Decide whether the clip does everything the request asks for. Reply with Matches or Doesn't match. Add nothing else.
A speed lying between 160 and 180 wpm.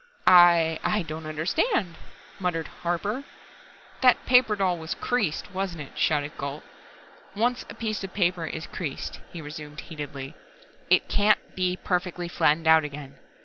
Doesn't match